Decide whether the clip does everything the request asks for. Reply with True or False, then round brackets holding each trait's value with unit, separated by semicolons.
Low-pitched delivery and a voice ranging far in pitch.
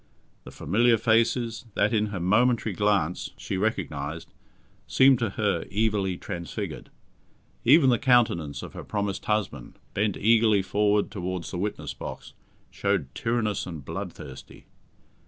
False (105 Hz; 3.9 semitones)